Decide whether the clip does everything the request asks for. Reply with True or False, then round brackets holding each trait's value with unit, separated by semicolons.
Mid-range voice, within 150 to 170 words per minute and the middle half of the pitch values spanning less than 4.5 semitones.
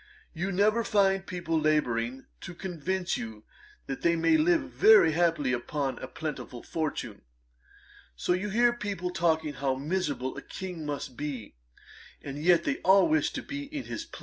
False (170 Hz; 165 wpm; 5.5 semitones)